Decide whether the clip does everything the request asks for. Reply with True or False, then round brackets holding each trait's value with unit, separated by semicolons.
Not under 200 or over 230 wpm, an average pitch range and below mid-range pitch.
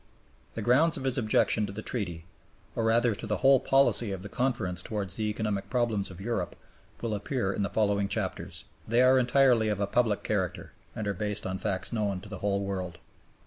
True (205 wpm; 3.3 semitones; 105 Hz)